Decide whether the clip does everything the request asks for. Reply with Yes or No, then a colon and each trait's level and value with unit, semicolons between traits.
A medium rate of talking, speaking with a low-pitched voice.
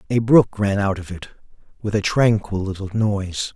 Yes: average, 185 wpm; low, 100 Hz